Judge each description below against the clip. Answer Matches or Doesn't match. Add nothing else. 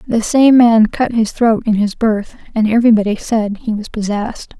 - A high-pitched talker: Matches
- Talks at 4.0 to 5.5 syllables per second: Matches